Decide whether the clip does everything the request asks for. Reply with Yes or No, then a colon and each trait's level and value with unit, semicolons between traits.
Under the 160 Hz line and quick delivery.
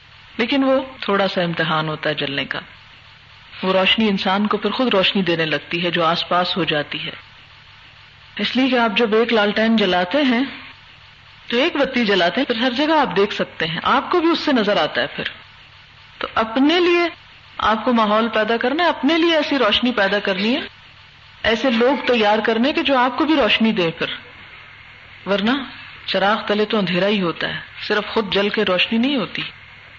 No: high, 210 Hz; fast, 195 wpm